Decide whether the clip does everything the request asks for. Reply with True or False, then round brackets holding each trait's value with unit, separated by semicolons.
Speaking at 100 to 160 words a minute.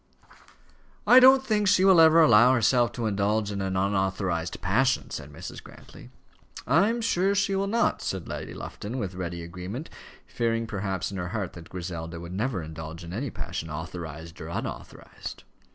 False (170 wpm)